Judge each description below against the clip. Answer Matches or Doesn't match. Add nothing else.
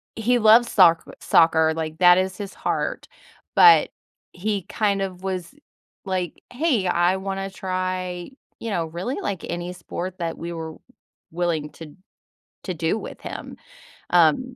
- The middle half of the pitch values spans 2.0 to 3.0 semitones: Matches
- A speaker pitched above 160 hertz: Matches